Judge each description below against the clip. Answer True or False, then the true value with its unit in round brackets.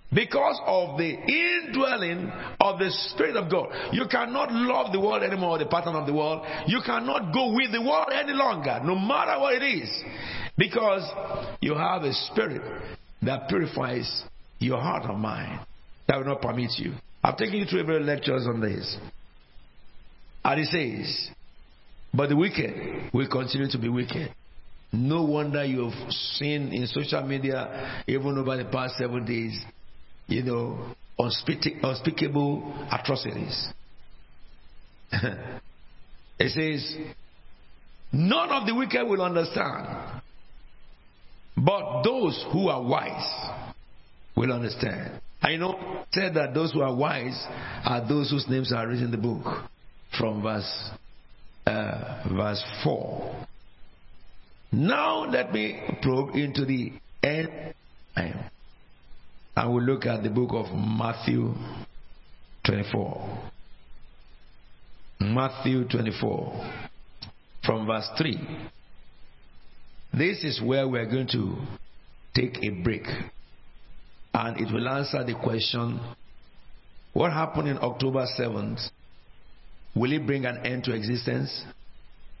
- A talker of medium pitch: False (130 Hz)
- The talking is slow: True (125 wpm)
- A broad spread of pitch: True (5.7 semitones)